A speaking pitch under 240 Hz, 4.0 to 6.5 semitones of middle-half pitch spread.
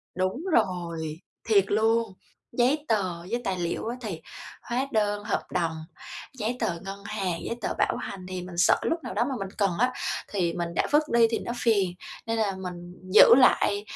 Yes: high, 205 Hz; average, 4.3 semitones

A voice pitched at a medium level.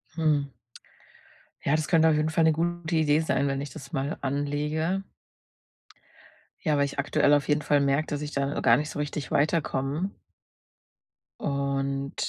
Yes: medium, 145 Hz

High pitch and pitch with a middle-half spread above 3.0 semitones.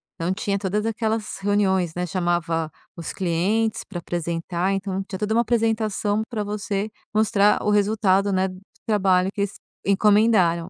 No: high, 200 Hz; narrow, 2.6 semitones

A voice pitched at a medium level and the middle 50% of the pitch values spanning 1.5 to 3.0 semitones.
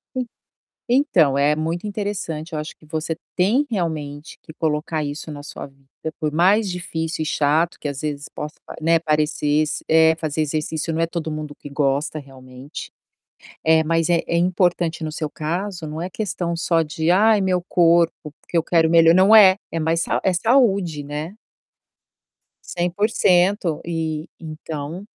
Yes: medium, 160 Hz; average, 2.7 semitones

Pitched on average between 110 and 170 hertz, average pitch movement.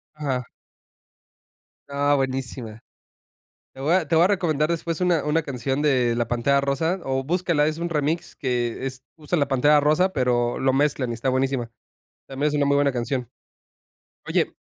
Yes: medium, 140 Hz; average, 3.1 semitones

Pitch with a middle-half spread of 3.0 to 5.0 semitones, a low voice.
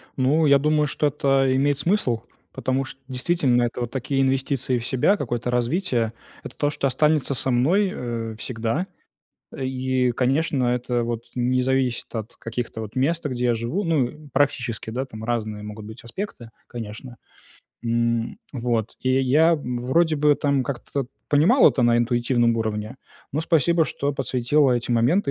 Yes: average, 3.3 semitones; low, 130 Hz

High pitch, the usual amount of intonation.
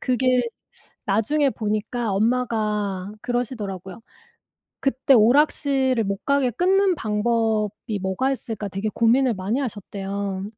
Yes: high, 225 Hz; average, 4.0 semitones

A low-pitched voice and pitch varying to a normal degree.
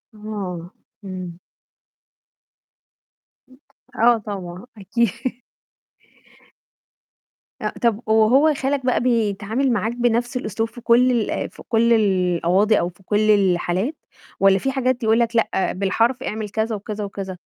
No: high, 215 Hz; average, 3.5 semitones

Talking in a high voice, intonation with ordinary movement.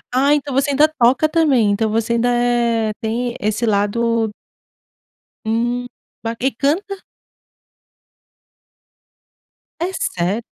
Yes: high, 240 Hz; average, 3.6 semitones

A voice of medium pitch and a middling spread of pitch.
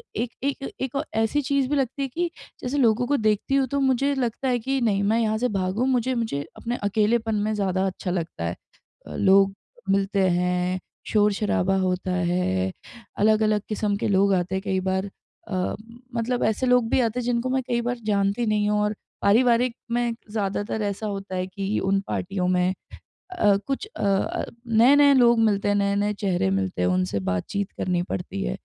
No: high, 210 Hz; average, 4.1 semitones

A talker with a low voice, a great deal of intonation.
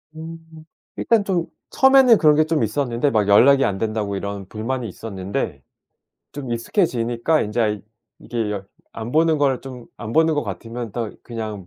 Yes: low, 120 Hz; wide, 6.2 semitones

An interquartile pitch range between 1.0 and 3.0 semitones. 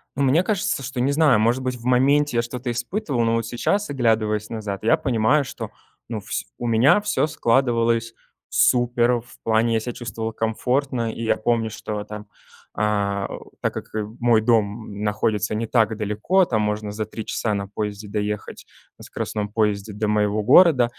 Yes: average, 2.7 semitones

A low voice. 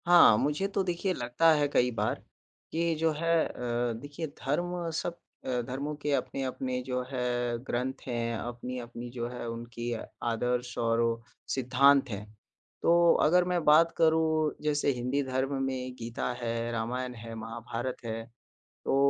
Yes: low, 130 Hz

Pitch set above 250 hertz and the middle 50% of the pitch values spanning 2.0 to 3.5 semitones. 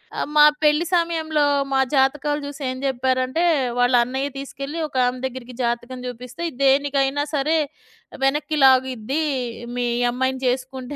Yes: very high, 265 Hz; narrow, 2.4 semitones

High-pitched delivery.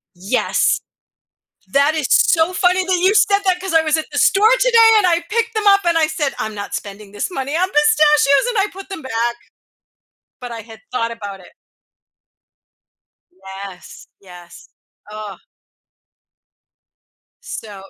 Yes: very high, 300 Hz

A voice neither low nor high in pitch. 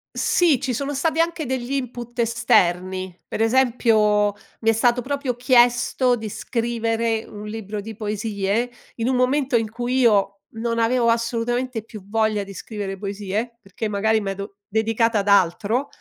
No: high, 225 Hz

